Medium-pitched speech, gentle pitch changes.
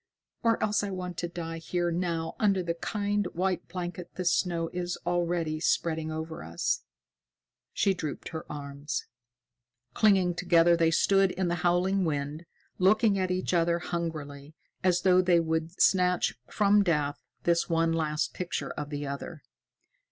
Yes: medium, 175 Hz; narrow, 2.3 semitones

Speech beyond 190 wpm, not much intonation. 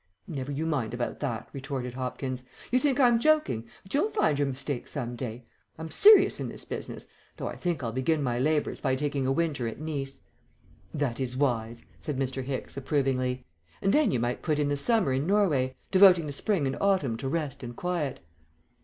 No: average, 200 wpm; average, 4.2 semitones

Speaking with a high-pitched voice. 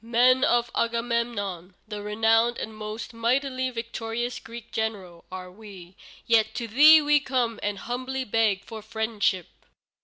Yes: high, 230 Hz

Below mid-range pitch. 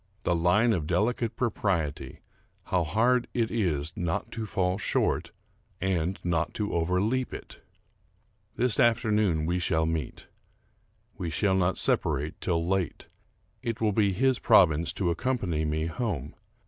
Yes: very low, 90 Hz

